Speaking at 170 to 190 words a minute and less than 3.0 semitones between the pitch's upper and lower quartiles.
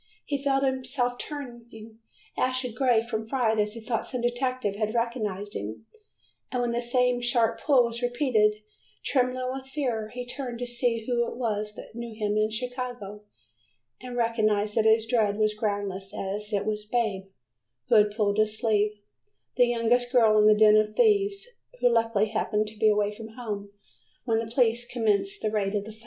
Yes: average, 185 wpm; narrow, 2.5 semitones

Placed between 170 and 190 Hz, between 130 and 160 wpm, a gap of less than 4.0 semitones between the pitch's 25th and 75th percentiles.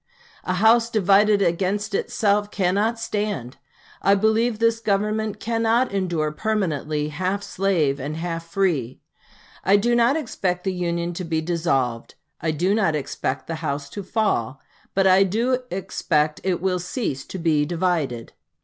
No: medium, 185 Hz; average, 150 wpm; average, 4.8 semitones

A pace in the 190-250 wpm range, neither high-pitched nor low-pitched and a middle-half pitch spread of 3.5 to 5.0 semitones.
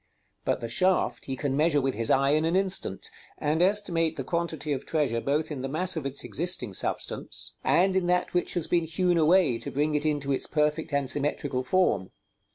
Yes: fast, 205 wpm; medium, 150 Hz; average, 4.1 semitones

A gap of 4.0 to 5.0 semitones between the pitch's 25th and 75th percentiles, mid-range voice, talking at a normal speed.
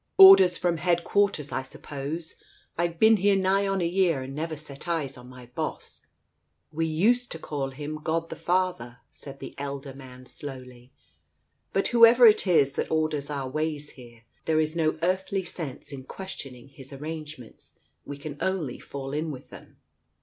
Yes: average, 4.6 semitones; medium, 155 Hz; average, 170 wpm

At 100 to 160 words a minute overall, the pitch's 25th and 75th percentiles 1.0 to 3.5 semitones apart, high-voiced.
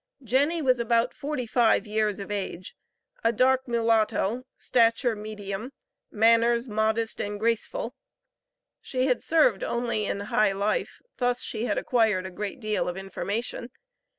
Yes: average, 140 wpm; average, 2.8 semitones; high, 230 Hz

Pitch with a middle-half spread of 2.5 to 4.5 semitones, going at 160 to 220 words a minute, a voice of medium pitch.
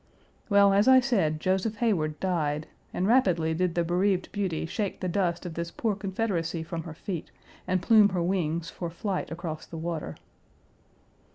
Yes: average, 3.4 semitones; average, 170 wpm; medium, 180 Hz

